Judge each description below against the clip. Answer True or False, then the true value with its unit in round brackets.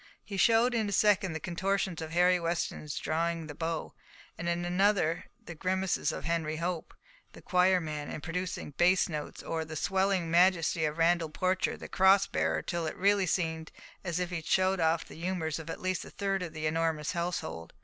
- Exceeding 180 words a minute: True (200 wpm)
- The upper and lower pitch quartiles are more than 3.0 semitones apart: False (2.6 semitones)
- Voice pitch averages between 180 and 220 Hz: False (170 Hz)